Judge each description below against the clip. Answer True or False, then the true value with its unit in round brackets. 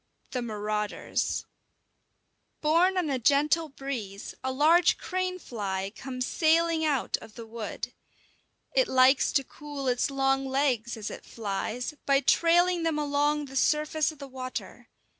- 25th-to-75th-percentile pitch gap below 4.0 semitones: False (4.3 semitones)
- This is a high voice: True (275 Hz)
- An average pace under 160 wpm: True (145 wpm)